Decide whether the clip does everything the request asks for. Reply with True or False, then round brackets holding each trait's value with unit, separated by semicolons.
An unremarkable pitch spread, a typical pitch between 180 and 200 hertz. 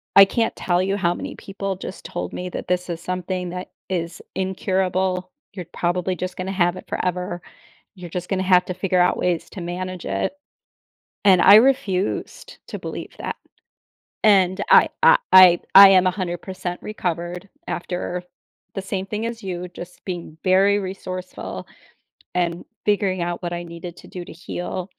False (1.4 semitones; 185 Hz)